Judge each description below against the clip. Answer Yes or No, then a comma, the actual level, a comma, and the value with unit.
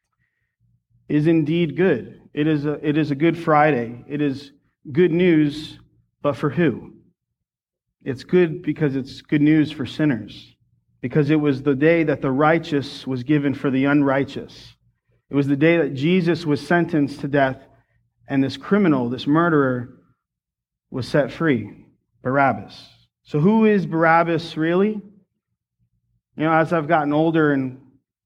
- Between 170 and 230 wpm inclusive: No, average, 150 wpm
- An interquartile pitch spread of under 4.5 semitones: Yes, average, 3.8 semitones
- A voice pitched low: No, medium, 145 Hz